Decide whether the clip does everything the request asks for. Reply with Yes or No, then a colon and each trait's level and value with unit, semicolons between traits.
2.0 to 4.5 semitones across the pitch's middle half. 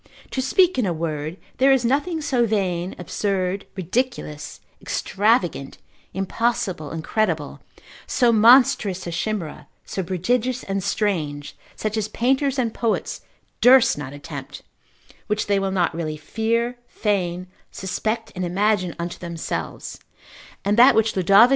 No: average, 5.1 semitones